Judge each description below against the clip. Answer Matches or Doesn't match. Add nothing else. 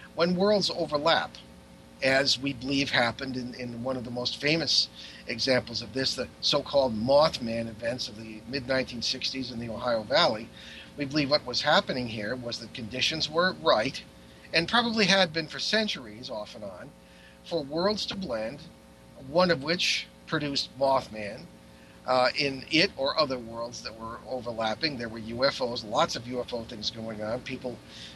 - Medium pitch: Doesn't match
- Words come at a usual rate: Matches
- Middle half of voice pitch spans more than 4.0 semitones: Matches